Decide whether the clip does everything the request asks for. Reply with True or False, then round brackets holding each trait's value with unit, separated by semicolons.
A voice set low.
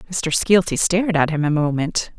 False (165 Hz)